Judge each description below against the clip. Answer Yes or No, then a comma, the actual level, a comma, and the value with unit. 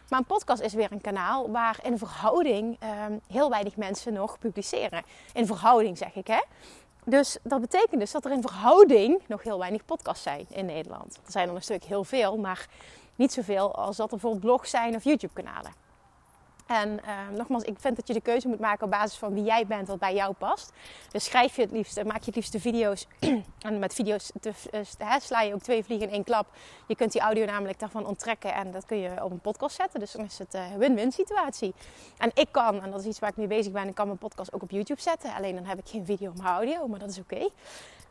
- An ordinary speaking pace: No, fast, 240 wpm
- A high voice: Yes, high, 215 Hz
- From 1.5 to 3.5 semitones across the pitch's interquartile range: Yes, average, 2.9 semitones